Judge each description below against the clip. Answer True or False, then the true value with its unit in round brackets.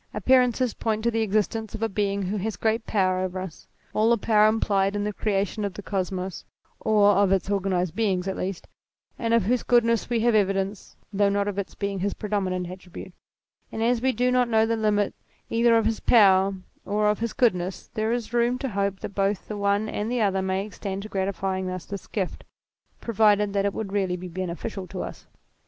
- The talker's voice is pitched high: True (205 Hz)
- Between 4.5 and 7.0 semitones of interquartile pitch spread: False (2.6 semitones)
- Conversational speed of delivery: False (210 wpm)